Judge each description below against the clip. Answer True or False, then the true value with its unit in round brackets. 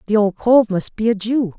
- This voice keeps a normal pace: False (265 wpm)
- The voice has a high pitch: True (215 Hz)